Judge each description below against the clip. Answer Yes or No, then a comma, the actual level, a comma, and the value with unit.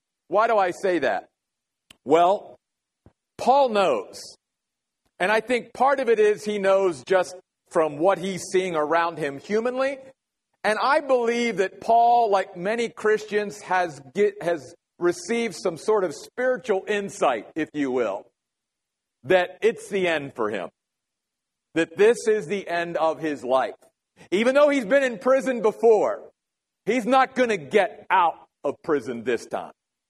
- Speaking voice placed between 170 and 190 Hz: No, high, 205 Hz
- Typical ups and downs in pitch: Yes, average, 5.0 semitones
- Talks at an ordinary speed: Yes, average, 150 wpm